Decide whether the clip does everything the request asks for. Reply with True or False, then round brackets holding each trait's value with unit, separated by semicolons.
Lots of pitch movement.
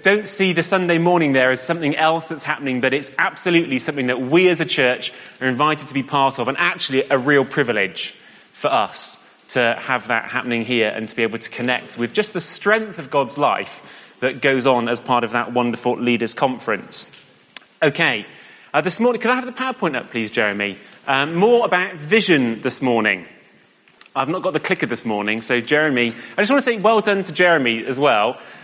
True (6.3 semitones)